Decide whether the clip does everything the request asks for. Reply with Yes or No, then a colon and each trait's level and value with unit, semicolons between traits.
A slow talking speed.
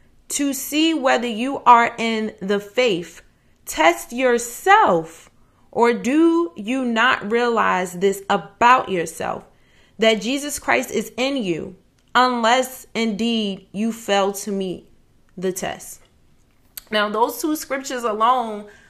Yes: slow, 115 wpm